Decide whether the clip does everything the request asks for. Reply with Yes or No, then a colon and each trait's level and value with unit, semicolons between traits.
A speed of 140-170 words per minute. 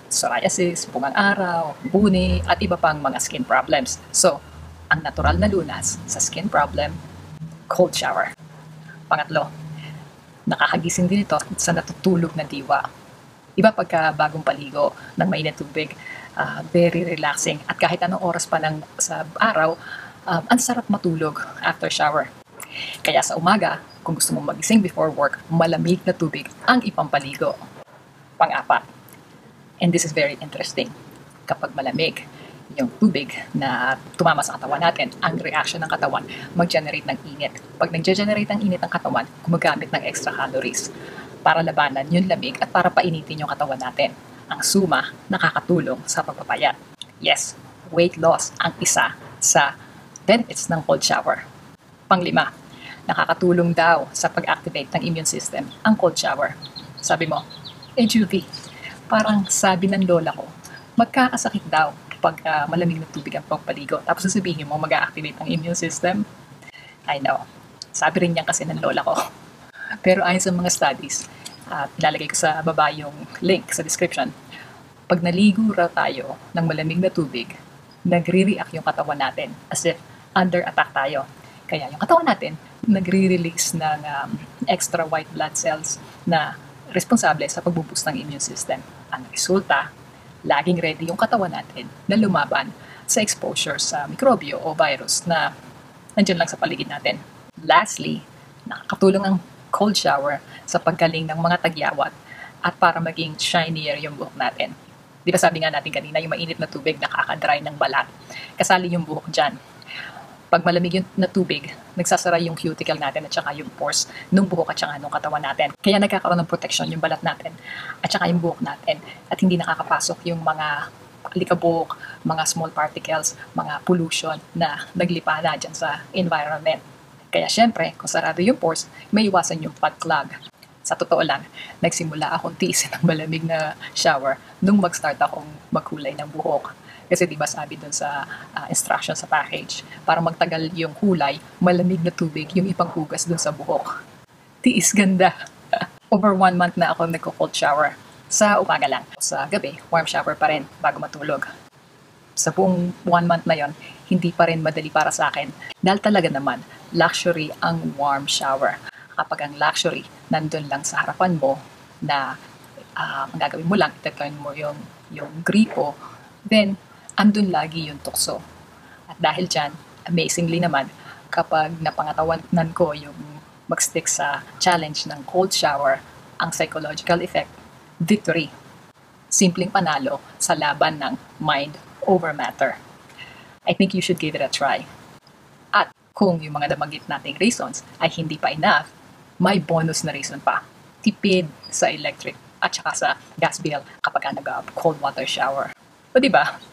Yes: average, 150 wpm